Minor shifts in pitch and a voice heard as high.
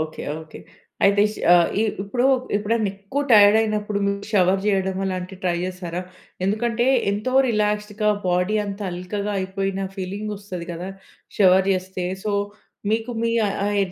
Yes: narrow, 2.2 semitones; high, 200 Hz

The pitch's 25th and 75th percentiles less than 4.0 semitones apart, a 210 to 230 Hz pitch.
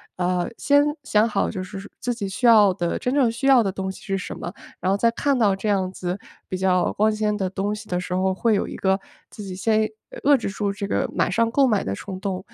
No: average, 3.1 semitones; high, 200 Hz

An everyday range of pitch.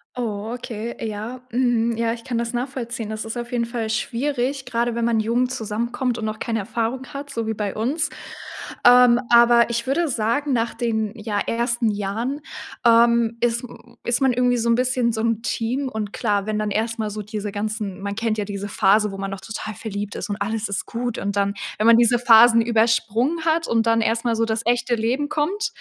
No: narrow, 2.0 semitones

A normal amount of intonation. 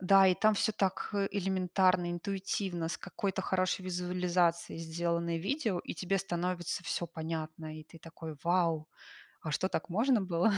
No: narrow, 2.3 semitones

